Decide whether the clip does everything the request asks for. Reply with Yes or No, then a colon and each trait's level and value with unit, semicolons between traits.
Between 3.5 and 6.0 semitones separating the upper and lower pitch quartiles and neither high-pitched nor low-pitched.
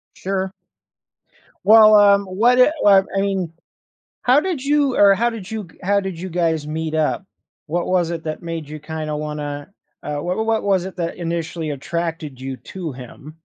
Yes: average, 4.4 semitones; medium, 175 Hz